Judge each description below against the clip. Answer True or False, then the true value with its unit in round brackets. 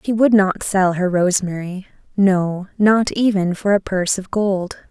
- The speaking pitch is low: False (195 Hz)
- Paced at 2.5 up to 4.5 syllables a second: True (4.3 syllables/s)